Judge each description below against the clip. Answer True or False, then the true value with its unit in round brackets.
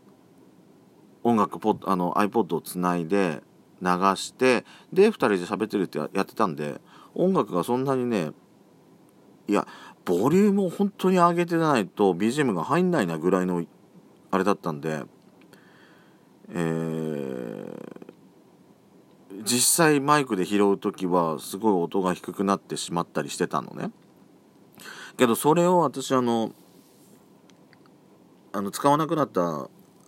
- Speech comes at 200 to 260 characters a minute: True (245 characters per minute)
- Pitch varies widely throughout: True (8.2 semitones)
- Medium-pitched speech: False (100 Hz)